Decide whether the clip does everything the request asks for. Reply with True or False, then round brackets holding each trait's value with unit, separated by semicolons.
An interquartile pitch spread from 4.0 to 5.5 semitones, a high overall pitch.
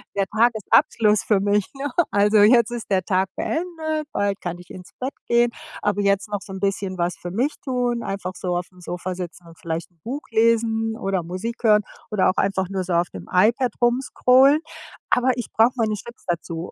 True (4.3 semitones; 205 Hz)